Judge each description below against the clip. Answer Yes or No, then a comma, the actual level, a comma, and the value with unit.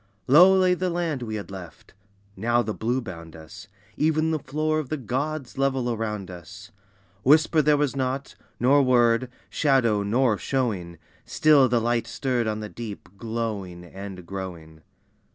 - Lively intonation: Yes, wide, 5.7 semitones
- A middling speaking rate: Yes, average, 155 wpm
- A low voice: Yes, low, 120 Hz